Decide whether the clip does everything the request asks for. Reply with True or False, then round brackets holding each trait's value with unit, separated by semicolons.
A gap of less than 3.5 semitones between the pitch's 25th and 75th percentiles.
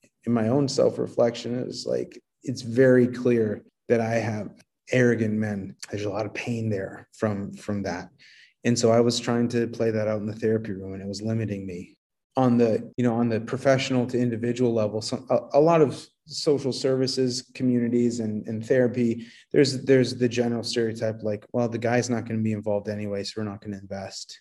True (2.4 semitones)